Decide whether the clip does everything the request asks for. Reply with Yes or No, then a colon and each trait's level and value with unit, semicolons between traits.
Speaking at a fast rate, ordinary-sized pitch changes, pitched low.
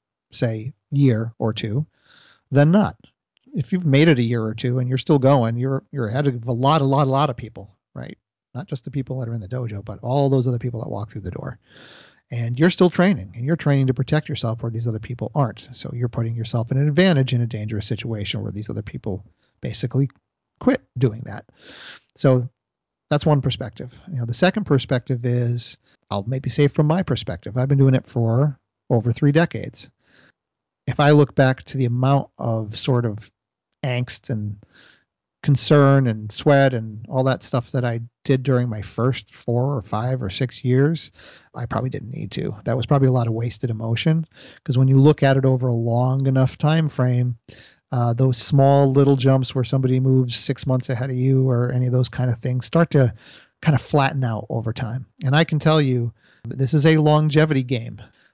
Yes: fast, 210 wpm; average, 3.1 semitones; low, 130 Hz